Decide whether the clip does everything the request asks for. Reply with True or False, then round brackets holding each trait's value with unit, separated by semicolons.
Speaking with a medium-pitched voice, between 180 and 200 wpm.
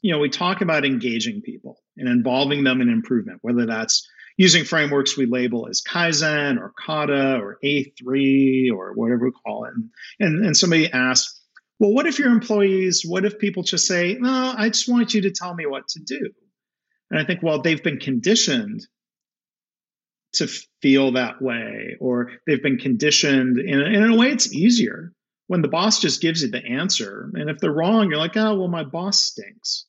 True (165 Hz; 190 wpm)